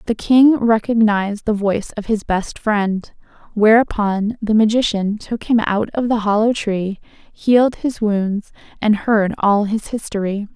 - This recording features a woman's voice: Yes, female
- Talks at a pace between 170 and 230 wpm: No, average, 155 wpm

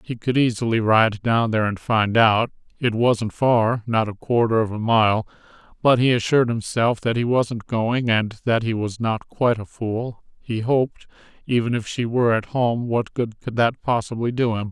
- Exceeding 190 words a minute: Yes, average, 200 wpm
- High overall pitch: No, low, 115 Hz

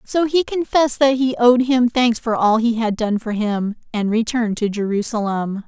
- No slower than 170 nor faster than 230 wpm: Yes, average, 200 wpm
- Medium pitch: No, high, 230 Hz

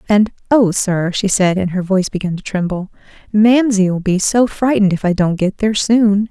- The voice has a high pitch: Yes, high, 200 Hz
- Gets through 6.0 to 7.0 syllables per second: No, 5.1 syllables/s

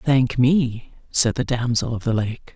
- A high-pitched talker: No, low, 125 Hz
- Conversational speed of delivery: Yes, average, 190 wpm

